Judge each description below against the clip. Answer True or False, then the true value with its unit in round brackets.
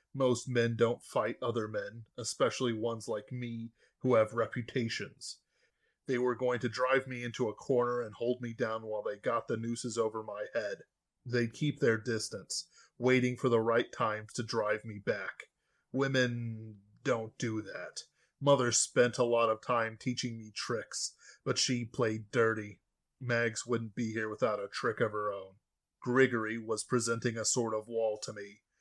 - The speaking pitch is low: True (115 Hz)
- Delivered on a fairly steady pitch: True (1.9 semitones)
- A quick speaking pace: False (175 wpm)